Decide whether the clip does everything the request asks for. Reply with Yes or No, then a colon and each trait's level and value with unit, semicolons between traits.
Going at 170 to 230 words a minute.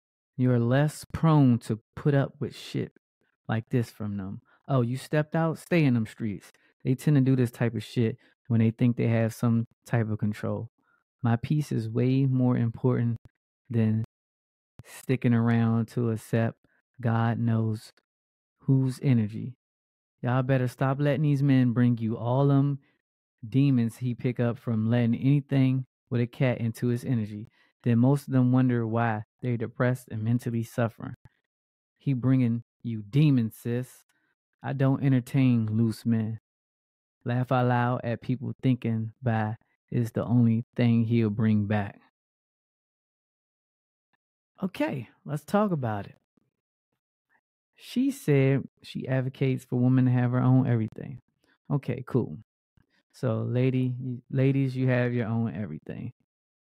No: average, 145 wpm